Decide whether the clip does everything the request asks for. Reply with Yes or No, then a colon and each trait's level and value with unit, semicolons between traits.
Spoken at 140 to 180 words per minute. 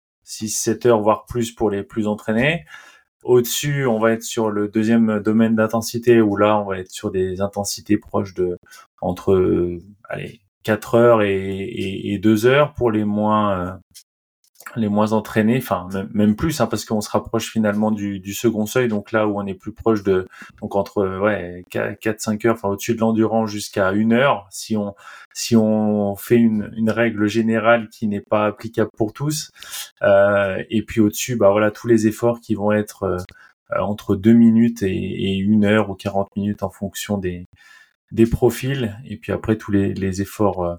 No: average, 195 wpm